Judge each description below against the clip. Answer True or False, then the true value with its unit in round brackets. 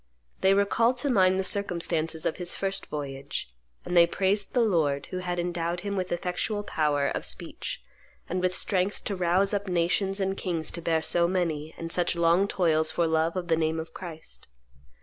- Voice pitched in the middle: True (175 Hz)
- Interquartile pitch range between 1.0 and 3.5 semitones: True (2.9 semitones)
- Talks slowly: False (190 wpm)